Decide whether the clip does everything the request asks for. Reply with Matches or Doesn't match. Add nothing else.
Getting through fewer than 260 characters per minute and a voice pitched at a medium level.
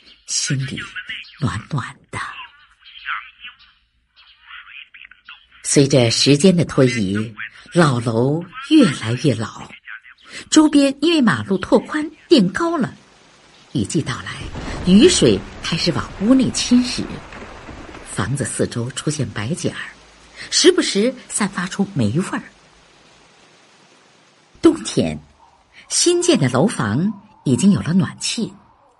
Matches